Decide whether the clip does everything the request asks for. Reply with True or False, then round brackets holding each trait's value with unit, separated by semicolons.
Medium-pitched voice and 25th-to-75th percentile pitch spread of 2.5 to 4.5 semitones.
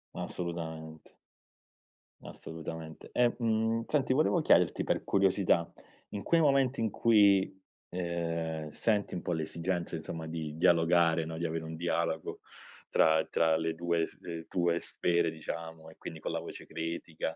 False (85 Hz; 2.8 semitones)